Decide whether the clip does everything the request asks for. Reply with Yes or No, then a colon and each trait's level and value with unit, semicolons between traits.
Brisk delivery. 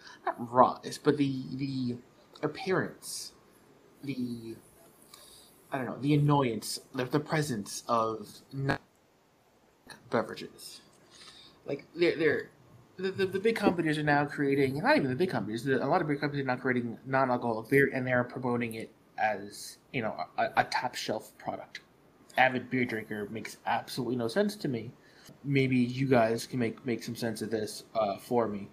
No: average, 160 wpm